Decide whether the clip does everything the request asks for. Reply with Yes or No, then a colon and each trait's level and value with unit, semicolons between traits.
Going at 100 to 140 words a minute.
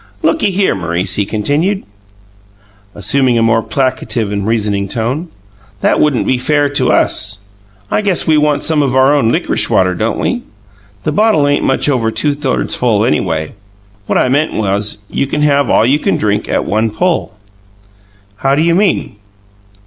No: average, 170 wpm